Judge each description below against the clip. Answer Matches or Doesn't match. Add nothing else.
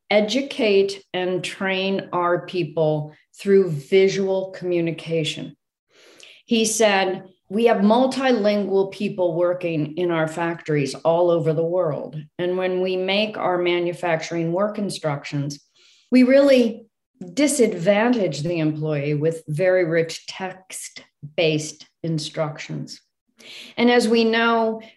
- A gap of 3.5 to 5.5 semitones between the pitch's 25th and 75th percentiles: Matches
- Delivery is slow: Matches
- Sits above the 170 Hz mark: Matches